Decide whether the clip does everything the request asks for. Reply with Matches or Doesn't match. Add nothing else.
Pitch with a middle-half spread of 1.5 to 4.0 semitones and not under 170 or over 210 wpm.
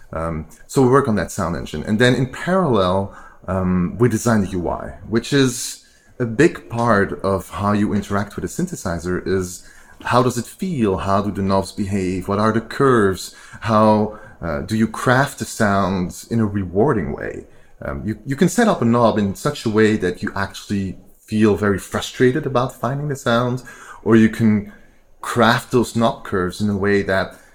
Matches